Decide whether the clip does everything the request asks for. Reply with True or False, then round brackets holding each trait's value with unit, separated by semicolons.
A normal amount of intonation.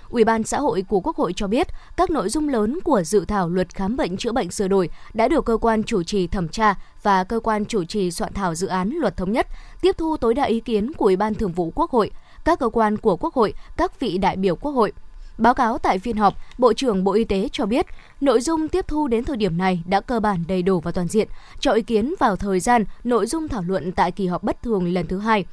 True (4.2 semitones)